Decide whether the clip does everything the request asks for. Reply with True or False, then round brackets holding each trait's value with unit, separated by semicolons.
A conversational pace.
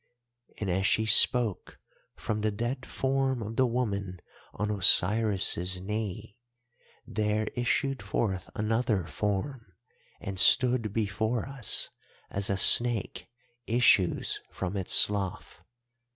False (110 wpm)